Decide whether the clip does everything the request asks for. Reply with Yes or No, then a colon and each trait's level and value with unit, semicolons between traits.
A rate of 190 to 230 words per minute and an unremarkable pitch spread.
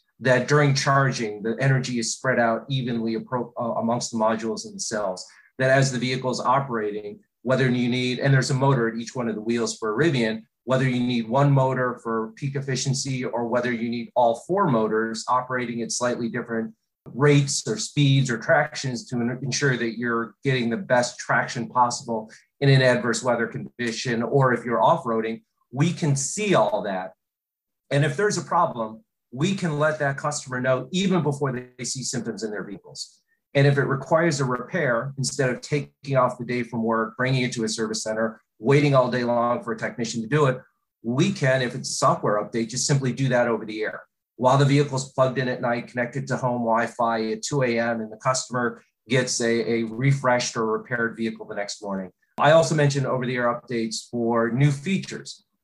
Yes: average, 200 wpm; average, 3.1 semitones